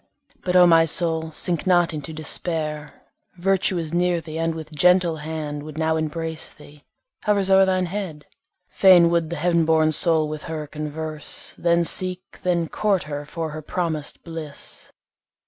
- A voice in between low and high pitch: Yes, medium, 165 Hz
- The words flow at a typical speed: Yes, average, 165 wpm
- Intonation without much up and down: Yes, narrow, 2.3 semitones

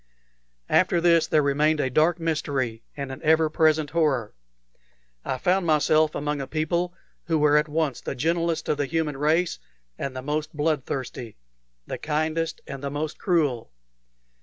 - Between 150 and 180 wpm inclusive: Yes, average, 160 wpm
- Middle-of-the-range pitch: Yes, medium, 155 Hz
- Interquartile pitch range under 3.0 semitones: Yes, narrow, 2.5 semitones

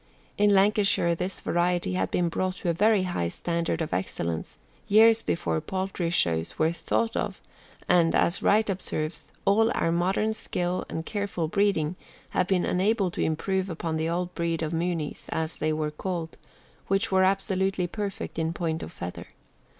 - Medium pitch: Yes, medium, 175 Hz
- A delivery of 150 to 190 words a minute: Yes, average, 165 wpm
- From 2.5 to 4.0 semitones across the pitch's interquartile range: Yes, average, 3.1 semitones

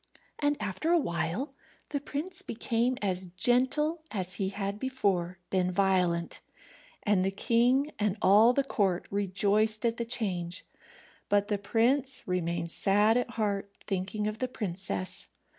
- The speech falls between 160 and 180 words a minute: No, average, 140 wpm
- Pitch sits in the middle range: No, high, 205 Hz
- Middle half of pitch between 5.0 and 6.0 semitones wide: No, average, 4.6 semitones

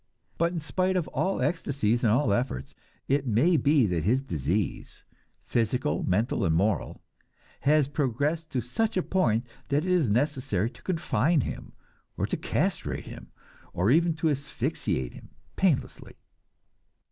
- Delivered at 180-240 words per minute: No, average, 145 wpm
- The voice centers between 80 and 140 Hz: Yes, low, 135 Hz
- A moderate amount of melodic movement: No, wide, 6.6 semitones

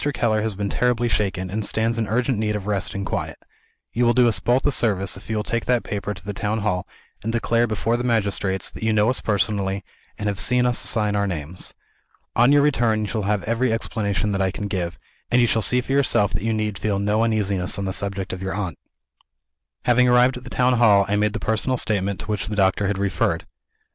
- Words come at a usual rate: No, fast, 240 wpm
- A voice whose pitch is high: No, low, 105 Hz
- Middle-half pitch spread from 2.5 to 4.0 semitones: Yes, average, 2.9 semitones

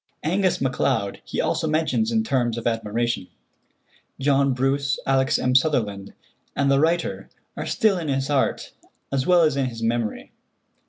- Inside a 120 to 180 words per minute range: Yes, average, 155 wpm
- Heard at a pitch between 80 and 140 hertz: Yes, low, 135 Hz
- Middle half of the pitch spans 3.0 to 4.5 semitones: Yes, average, 3.8 semitones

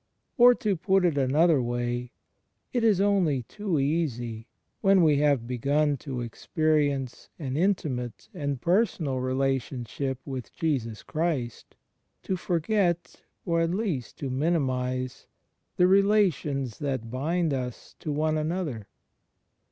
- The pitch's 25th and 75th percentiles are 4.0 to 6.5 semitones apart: Yes, average, 5.2 semitones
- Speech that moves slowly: Yes, slow, 125 wpm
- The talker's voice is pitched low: No, medium, 145 Hz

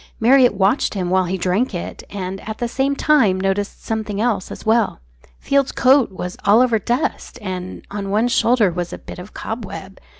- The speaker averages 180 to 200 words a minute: Yes, average, 190 wpm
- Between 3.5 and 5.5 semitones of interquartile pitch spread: Yes, average, 4.3 semitones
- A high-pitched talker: Yes, high, 205 Hz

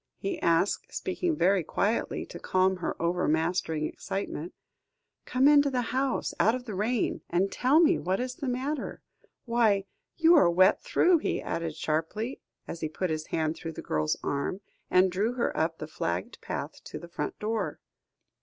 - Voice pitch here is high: Yes, high, 195 Hz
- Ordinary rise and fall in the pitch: No, wide, 7.3 semitones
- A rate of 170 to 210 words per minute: Yes, average, 175 wpm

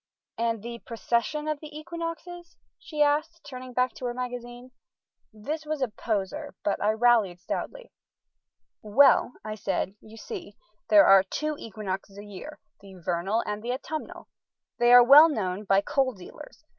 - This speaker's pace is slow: No, average, 155 wpm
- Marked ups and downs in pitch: Yes, wide, 6.3 semitones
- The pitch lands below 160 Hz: No, high, 245 Hz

